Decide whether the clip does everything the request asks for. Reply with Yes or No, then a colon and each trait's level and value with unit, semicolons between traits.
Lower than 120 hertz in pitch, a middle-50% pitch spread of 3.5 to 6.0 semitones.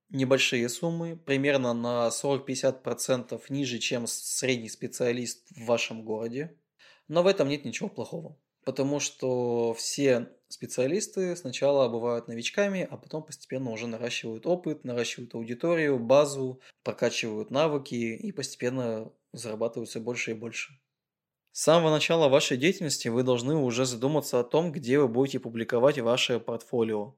No: low, 130 Hz; average, 3.8 semitones